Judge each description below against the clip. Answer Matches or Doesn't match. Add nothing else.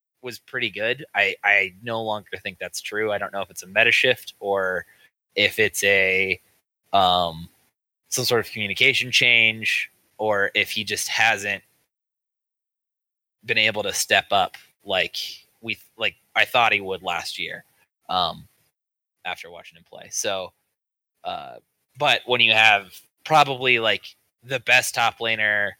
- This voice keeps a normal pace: Matches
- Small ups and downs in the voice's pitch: Doesn't match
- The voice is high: Doesn't match